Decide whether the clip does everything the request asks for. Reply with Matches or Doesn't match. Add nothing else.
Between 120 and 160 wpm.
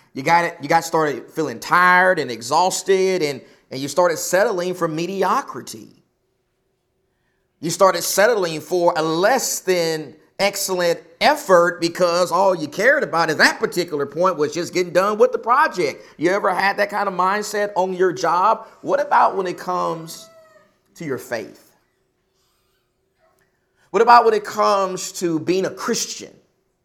Matches